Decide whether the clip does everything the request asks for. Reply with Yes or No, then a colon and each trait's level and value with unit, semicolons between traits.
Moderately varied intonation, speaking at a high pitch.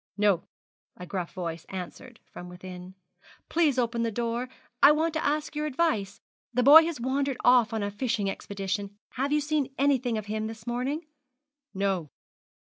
No: wide, 6.0 semitones; high, 235 Hz